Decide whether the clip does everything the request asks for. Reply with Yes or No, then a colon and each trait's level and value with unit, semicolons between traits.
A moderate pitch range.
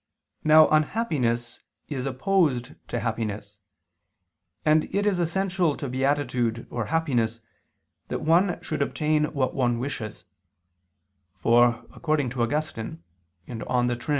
Yes: average, 4.7 semitones